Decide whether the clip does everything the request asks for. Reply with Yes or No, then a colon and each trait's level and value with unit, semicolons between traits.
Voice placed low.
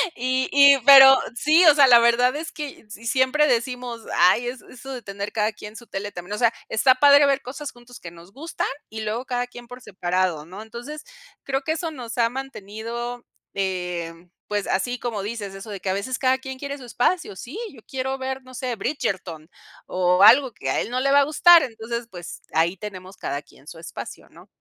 No: high, 240 Hz